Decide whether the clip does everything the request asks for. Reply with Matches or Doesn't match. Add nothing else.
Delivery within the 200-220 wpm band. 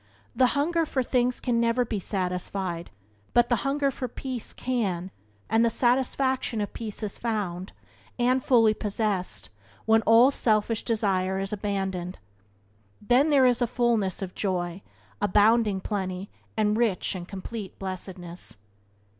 Doesn't match